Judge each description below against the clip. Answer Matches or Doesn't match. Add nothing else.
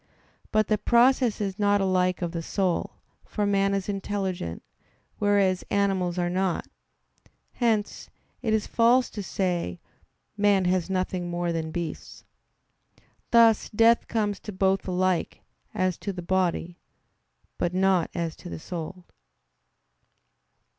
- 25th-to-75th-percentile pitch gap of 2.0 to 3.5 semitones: Matches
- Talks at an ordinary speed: Doesn't match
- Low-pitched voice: Doesn't match